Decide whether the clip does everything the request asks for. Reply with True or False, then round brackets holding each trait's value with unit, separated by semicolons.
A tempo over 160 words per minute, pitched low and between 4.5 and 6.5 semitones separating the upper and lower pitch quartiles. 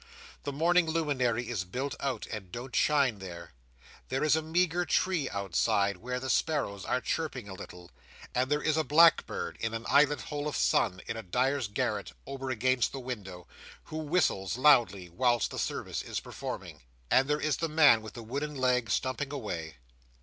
True (180 wpm; 130 Hz; 5.5 semitones)